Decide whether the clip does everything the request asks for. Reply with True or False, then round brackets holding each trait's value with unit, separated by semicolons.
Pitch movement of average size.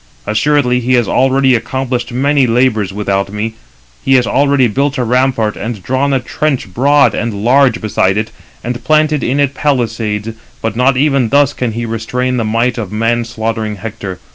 True (3.3 semitones)